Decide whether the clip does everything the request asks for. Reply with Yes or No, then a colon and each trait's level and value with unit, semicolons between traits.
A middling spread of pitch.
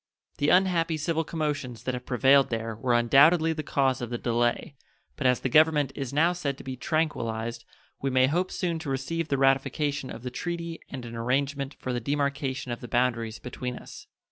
Yes: average, 3.8 semitones